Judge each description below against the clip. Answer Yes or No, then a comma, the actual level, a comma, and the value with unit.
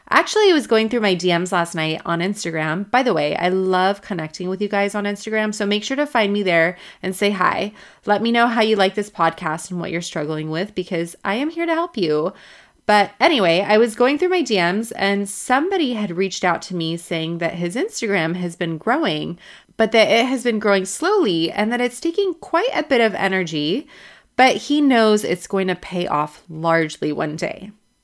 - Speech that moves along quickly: Yes, fast, 215 wpm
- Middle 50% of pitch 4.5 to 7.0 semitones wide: Yes, wide, 5.4 semitones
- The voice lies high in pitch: Yes, high, 200 Hz